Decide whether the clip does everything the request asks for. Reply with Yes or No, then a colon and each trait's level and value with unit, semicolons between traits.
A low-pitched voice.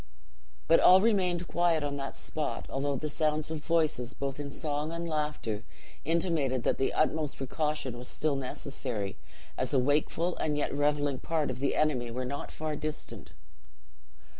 No: medium, 150 Hz